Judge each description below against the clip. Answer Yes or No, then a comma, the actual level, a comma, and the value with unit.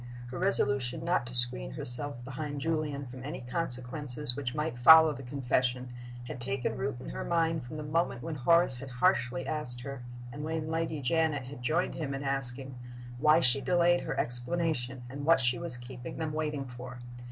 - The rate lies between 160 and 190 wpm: Yes, average, 185 wpm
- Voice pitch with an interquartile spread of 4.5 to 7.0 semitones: No, average, 4.0 semitones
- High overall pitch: No, low, 135 Hz